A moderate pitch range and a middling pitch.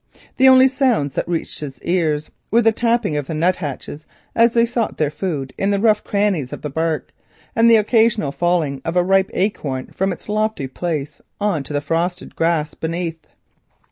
No: wide, 5.9 semitones; medium, 175 Hz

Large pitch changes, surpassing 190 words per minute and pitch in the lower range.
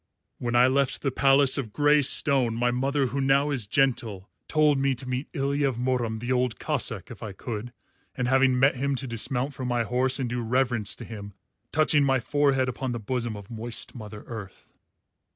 No: narrow, 2.6 semitones; average, 200 wpm; low, 125 Hz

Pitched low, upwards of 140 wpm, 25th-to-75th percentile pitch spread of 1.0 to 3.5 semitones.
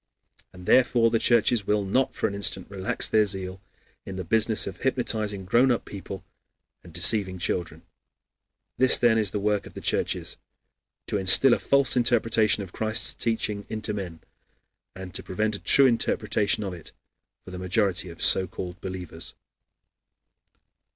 Yes: low, 100 Hz; average, 160 wpm; average, 3.2 semitones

